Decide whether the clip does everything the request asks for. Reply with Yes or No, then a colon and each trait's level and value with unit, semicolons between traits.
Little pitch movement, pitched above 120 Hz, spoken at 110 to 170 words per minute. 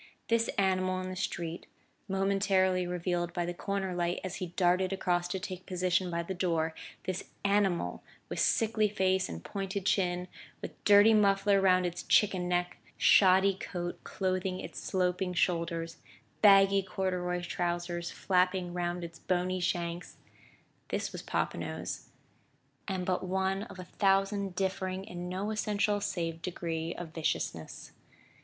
Yes: narrow, 1.7 semitones; medium, 185 Hz; average, 140 wpm